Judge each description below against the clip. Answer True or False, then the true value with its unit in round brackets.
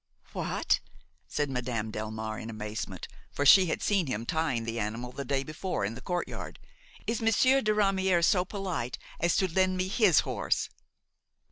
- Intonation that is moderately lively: False (8.6 semitones)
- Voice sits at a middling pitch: True (155 Hz)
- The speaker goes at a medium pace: True (165 wpm)